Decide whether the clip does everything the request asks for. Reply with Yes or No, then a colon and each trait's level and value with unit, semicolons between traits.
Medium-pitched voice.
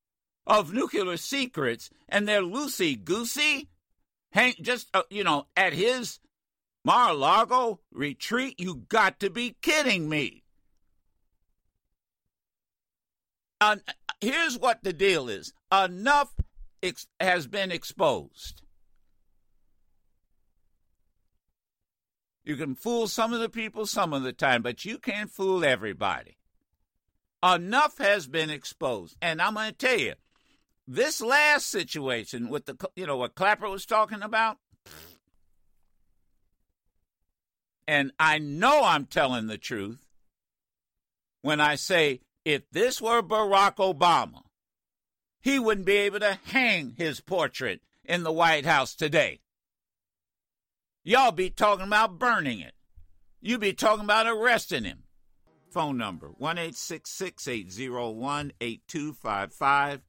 Yes: medium, 170 Hz